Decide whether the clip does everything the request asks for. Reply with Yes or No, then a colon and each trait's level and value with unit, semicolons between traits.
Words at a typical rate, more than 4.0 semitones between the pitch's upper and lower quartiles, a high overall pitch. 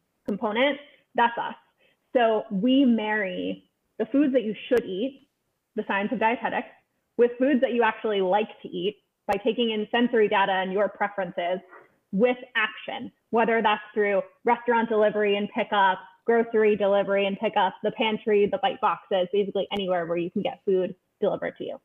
No: average, 165 wpm; average, 3.1 semitones; high, 215 Hz